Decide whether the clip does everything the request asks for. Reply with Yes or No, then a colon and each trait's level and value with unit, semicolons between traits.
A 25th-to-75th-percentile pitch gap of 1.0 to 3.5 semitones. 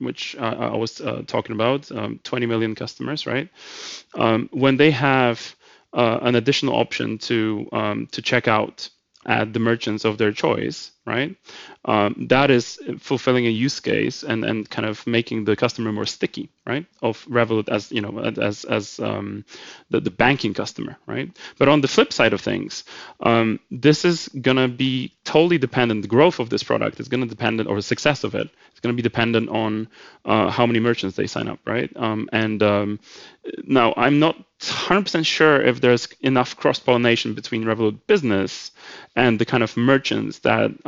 Yes: average, 3.0 semitones